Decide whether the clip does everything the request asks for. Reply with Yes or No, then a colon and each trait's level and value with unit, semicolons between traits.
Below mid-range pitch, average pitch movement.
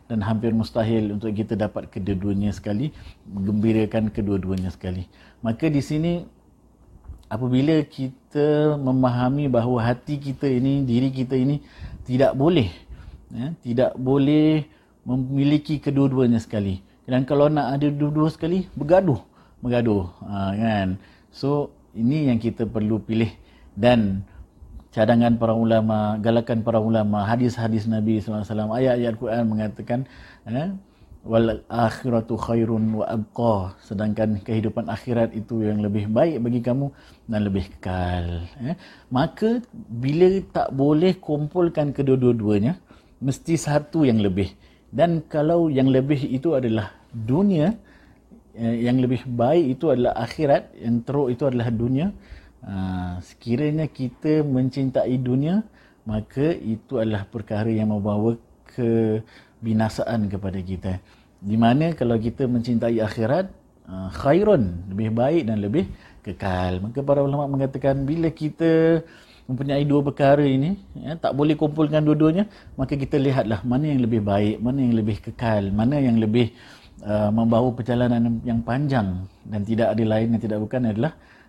Yes: low, 120 Hz; average, 4.4 semitones